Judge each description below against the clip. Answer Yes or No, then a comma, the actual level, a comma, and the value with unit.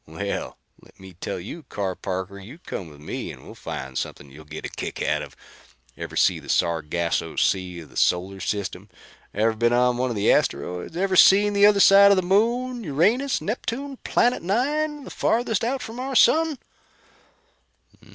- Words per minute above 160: Yes, average, 180 wpm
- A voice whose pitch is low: Yes, low, 130 Hz